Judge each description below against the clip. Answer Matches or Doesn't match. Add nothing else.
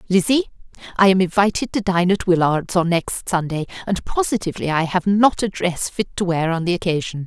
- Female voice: Matches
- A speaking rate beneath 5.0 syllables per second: Doesn't match